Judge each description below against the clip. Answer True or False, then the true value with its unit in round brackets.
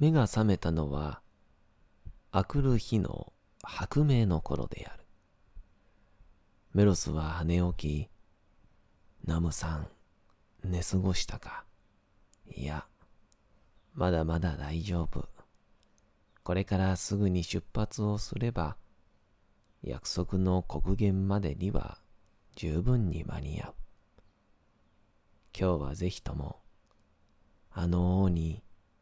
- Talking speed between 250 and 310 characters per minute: False (180 characters per minute)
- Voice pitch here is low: True (95 Hz)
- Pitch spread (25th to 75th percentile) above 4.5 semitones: False (3.7 semitones)